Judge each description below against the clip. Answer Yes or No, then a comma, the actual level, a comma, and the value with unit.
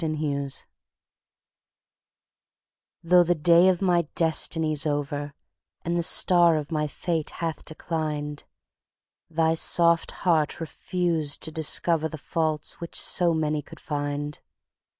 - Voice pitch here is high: No, medium, 160 Hz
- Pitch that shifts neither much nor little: No, narrow, 2.1 semitones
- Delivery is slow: Yes, slow, 110 wpm